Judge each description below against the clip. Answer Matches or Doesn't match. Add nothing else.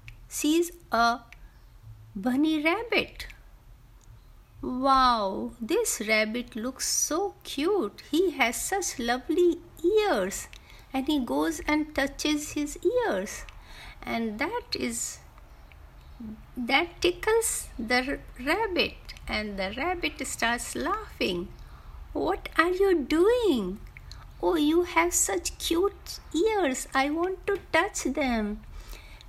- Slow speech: Matches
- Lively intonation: Matches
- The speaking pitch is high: Matches